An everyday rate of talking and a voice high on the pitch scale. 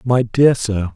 No: average, 190 wpm; low, 115 Hz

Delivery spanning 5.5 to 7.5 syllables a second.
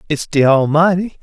No: 5.0 syllables/s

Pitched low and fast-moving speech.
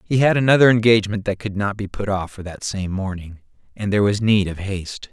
Yes: low, 100 Hz; fast, 235 wpm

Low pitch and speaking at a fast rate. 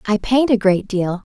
No: high, 210 Hz; fast, 225 wpm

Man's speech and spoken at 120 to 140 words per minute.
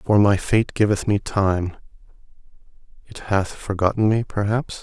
Yes: male; slow, 135 wpm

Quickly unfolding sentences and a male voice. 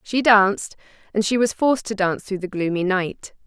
No: fast, 210 wpm; female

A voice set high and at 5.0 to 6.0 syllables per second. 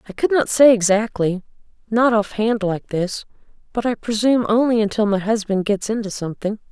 Yes: high, 215 Hz; 5.5 syllables/s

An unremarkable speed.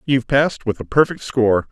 No: fast, 210 wpm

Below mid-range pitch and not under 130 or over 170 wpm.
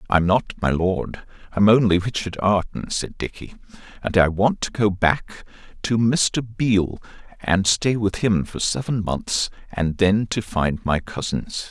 Yes: low, 100 Hz; average, 165 wpm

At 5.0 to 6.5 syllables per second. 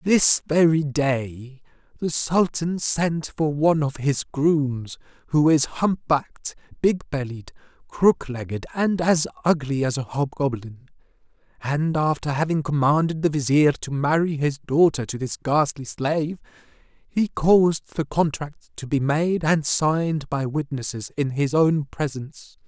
No: 4.1 syllables/s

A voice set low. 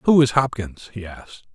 Yes: low, 120 Hz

